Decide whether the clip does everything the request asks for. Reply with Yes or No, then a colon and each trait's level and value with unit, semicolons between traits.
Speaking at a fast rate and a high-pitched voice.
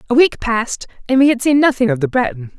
Yes: fast, 255 wpm; very high, 255 Hz